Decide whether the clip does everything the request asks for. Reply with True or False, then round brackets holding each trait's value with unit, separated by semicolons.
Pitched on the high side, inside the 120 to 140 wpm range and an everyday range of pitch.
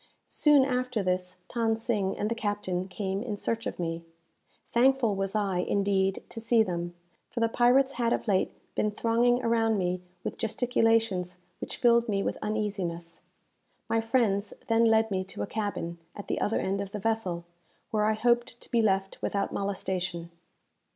False (210 Hz; 170 wpm; 3.2 semitones)